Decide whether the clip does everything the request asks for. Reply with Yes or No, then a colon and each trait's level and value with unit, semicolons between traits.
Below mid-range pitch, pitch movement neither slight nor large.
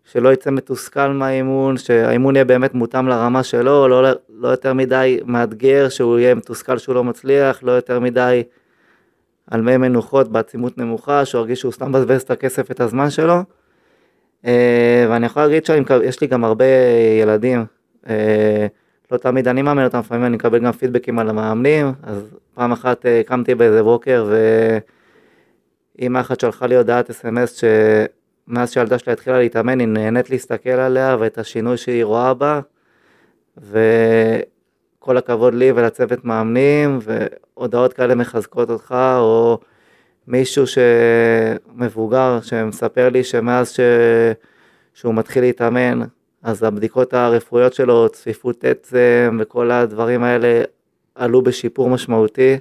No: low, 125 Hz; narrow, 1.9 semitones